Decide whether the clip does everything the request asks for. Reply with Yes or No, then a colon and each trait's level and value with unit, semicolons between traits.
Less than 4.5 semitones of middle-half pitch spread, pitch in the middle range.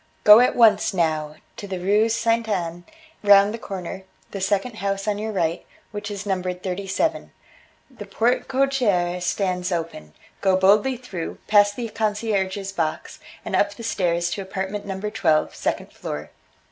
No: average, 2.8 semitones; high, 200 Hz